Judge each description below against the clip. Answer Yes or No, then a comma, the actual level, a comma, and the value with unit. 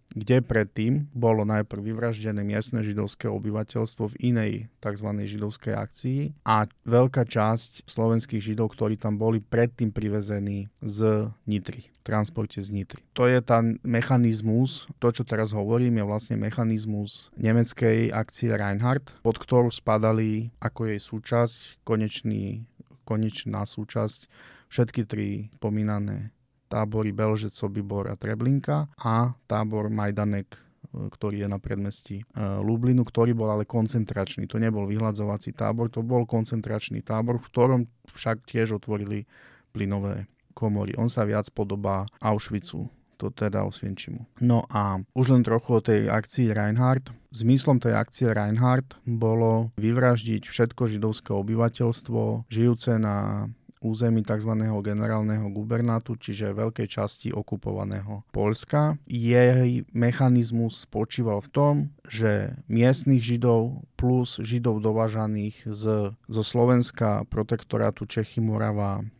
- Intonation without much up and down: Yes, narrow, 2.2 semitones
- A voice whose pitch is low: Yes, low, 110 Hz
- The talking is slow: No, average, 120 wpm